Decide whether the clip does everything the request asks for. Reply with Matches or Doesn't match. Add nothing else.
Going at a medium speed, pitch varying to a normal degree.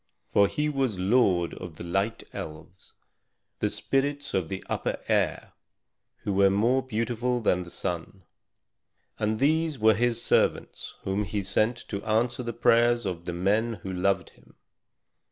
Matches